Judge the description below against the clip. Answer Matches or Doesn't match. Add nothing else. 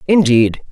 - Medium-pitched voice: Matches